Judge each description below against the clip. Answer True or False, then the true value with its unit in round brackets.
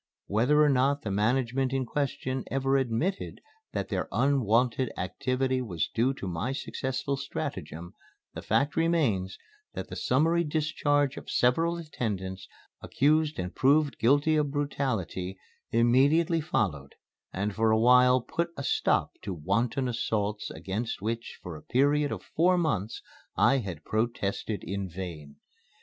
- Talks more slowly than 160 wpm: True (140 wpm)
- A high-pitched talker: False (125 Hz)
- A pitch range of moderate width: False (5.8 semitones)